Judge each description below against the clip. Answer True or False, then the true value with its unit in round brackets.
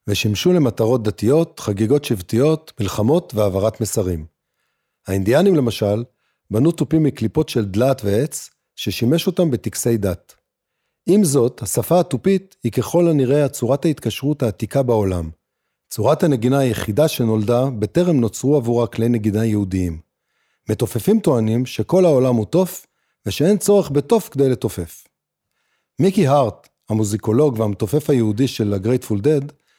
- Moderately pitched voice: False (120 Hz)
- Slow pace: False (120 wpm)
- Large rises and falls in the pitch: True (5.7 semitones)